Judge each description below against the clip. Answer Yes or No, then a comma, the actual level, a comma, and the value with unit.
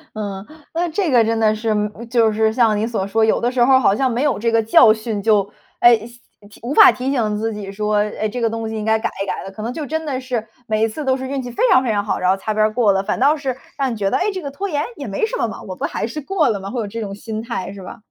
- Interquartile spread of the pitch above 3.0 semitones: Yes, average, 3.5 semitones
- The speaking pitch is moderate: No, high, 225 Hz